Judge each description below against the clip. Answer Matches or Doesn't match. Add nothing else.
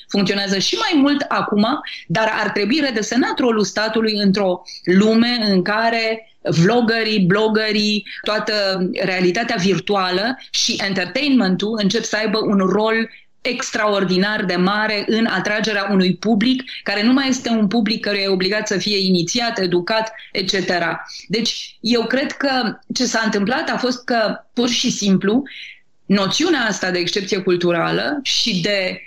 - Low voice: Doesn't match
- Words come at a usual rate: Matches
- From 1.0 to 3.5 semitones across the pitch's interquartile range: Matches